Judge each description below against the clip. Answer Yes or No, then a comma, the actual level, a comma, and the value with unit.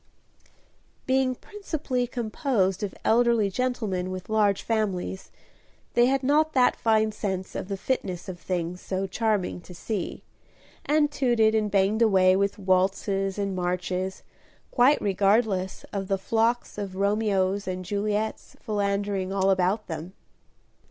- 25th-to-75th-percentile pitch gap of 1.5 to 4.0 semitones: Yes, average, 3.2 semitones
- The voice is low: No, high, 200 Hz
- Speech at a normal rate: No, slow, 130 wpm